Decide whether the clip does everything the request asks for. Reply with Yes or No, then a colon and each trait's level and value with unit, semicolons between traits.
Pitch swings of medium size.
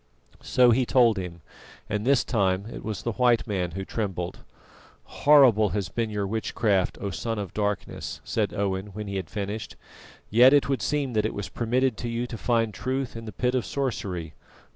Yes: average, 3.7 semitones